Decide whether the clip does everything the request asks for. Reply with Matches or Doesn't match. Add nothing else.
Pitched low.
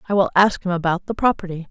Doesn't match